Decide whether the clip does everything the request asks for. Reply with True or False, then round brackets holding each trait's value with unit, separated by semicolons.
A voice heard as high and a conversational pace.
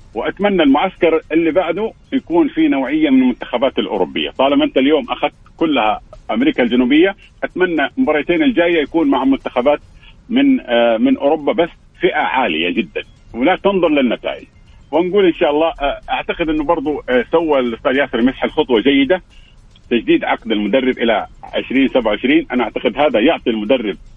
False (195 Hz; 140 wpm)